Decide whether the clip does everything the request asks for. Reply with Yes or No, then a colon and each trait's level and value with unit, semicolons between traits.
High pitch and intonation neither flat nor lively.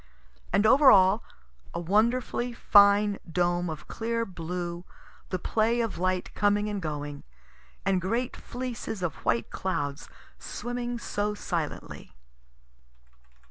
Yes: high, 200 Hz; average, 4.6 semitones